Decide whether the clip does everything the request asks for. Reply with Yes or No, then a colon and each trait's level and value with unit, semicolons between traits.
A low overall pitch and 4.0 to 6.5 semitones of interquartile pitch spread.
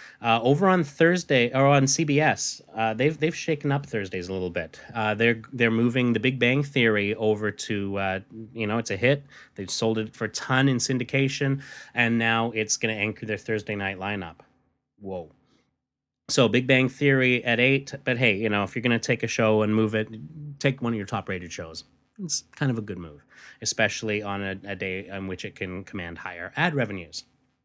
Yes: low, 115 Hz; average, 4.4 semitones